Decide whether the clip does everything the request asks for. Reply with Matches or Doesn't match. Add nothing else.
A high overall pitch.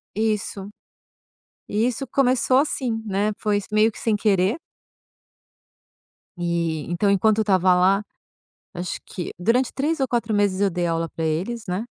Matches